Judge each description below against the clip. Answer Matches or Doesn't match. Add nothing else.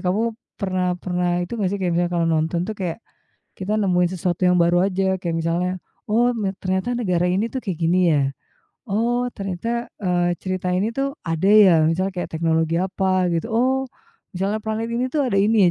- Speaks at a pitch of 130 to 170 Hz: Doesn't match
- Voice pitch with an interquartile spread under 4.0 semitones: Matches